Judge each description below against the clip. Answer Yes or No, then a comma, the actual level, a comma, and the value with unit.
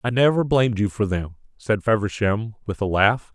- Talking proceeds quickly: No, average, 195 wpm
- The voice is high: No, low, 110 Hz